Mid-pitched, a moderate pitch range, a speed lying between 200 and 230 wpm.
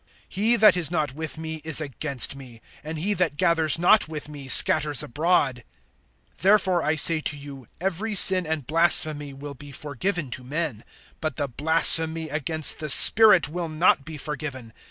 No: medium, 155 Hz; average, 3.0 semitones; average, 170 wpm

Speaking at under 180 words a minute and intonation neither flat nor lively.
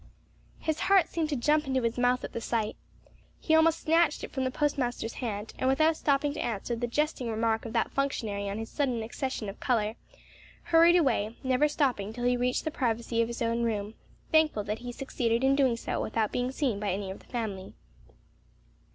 No: fast, 205 wpm; average, 4.3 semitones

